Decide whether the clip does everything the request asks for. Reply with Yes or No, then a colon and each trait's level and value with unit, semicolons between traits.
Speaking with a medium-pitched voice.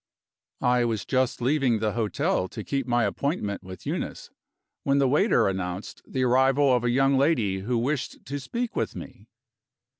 No: low, 125 Hz